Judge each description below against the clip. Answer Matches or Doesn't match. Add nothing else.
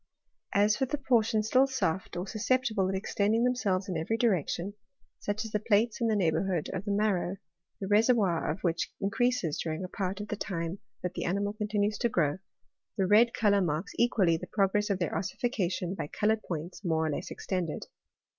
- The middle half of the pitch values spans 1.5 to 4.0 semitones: Matches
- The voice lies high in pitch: Matches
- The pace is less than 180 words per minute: Doesn't match